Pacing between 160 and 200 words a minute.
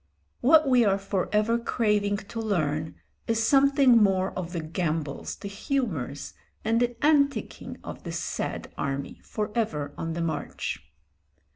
No: average, 145 wpm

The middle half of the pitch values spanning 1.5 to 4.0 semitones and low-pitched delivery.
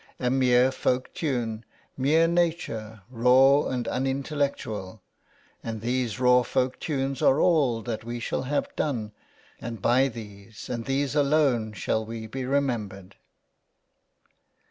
Yes: average, 3.4 semitones; low, 125 Hz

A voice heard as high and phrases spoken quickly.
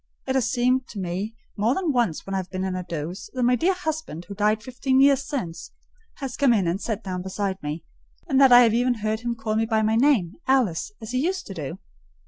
Yes: high, 225 Hz; fast, 245 wpm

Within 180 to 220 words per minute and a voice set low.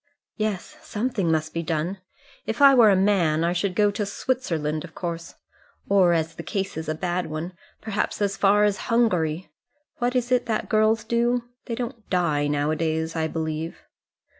No: average, 185 wpm; medium, 185 Hz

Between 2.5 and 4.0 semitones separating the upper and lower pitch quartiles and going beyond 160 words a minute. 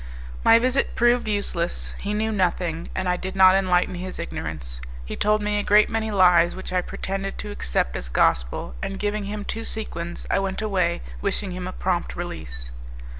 Yes: average, 3.3 semitones; average, 185 wpm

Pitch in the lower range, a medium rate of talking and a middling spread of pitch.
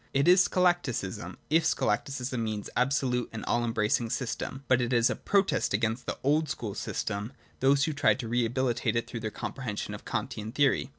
No: low, 125 Hz; fast, 210 wpm; average, 3.6 semitones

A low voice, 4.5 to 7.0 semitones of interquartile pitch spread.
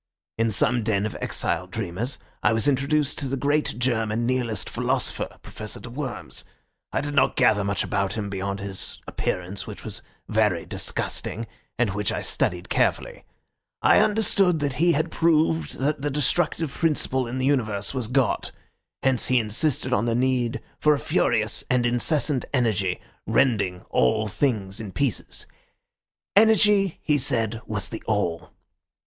Yes: low, 120 Hz; average, 5.2 semitones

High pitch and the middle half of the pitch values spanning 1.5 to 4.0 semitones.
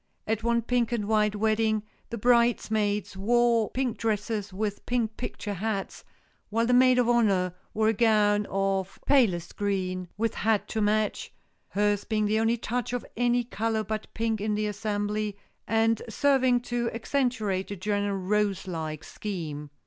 Yes: high, 215 Hz; narrow, 2.4 semitones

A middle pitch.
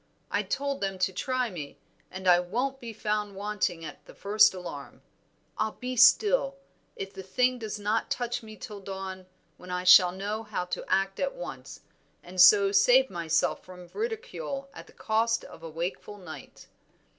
No: high, 205 Hz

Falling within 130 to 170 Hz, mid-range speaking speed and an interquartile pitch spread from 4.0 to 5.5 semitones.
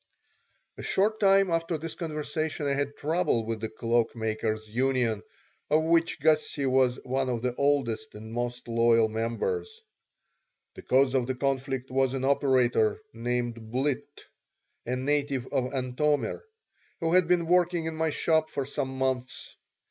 Yes: low, 135 Hz; average, 150 wpm; average, 4.6 semitones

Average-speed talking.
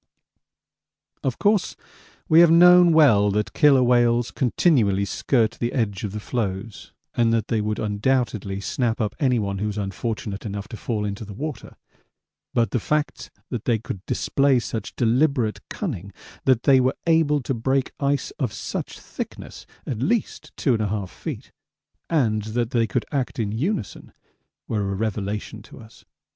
Yes: average, 160 wpm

